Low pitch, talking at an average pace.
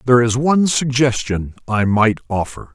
Yes: low, 120 Hz; average, 155 wpm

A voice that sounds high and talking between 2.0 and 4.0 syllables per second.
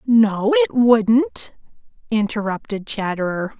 Yes: high, 225 Hz; 3.6 syllables/s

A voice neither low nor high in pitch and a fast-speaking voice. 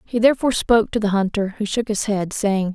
No: high, 210 Hz; fast, 240 wpm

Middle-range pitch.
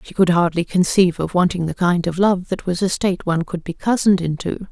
Yes: medium, 180 Hz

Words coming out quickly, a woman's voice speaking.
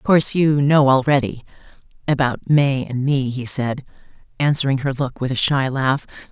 No: average, 160 wpm; female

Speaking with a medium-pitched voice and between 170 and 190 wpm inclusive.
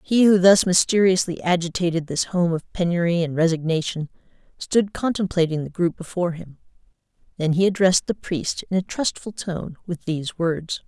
No: medium, 175 Hz; average, 160 wpm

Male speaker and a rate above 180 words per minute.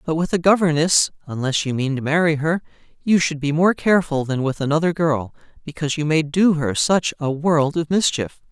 Yes: male; fast, 205 wpm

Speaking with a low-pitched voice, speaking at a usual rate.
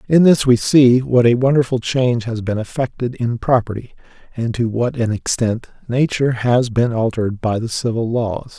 Yes: low, 120 Hz; average, 180 wpm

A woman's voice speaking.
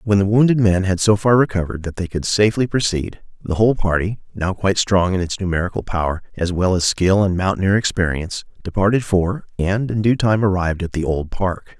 No: male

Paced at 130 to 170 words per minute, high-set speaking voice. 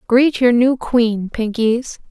Yes: average, 140 wpm; high, 240 Hz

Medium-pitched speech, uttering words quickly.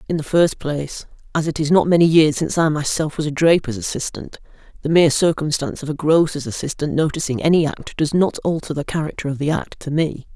Yes: medium, 155 Hz; fast, 215 wpm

